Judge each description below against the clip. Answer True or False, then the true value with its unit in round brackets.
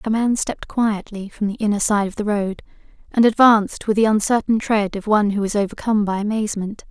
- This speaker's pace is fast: True (210 wpm)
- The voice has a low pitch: False (210 Hz)